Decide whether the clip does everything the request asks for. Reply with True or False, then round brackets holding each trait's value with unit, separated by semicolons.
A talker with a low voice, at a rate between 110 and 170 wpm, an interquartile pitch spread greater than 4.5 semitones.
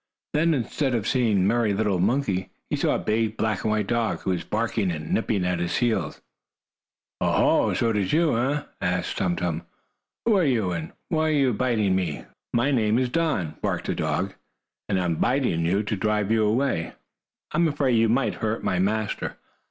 False (110 Hz; 205 wpm; 5.1 semitones)